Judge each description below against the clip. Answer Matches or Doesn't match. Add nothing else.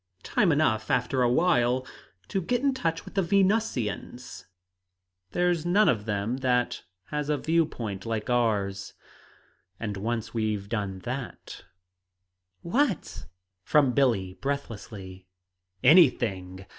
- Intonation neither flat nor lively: Doesn't match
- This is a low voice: Matches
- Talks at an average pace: Doesn't match